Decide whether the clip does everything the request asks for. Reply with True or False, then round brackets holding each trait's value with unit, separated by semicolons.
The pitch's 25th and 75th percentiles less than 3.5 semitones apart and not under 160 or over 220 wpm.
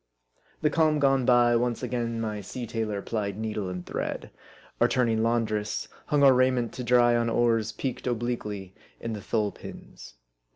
True (2.4 semitones; 165 wpm)